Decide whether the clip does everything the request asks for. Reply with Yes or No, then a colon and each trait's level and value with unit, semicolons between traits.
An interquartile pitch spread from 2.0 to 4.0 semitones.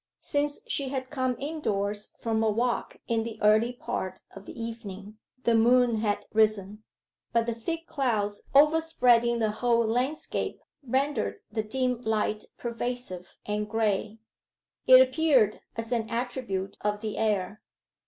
Yes: average, 3.1 semitones